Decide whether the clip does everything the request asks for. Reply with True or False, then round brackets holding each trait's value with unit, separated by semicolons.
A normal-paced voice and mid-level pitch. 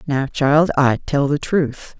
True (180 wpm; 145 Hz)